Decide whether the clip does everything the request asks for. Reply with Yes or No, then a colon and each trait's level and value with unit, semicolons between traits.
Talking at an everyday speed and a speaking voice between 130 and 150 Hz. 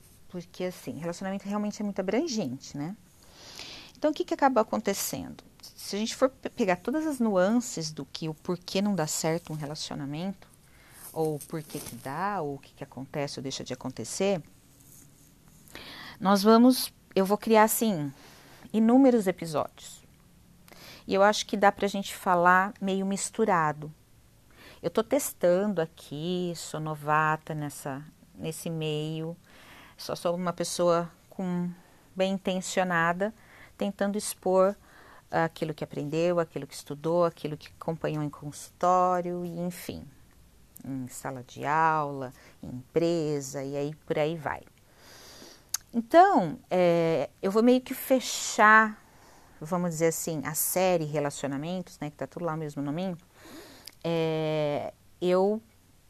No: average, 135 wpm; medium, 170 Hz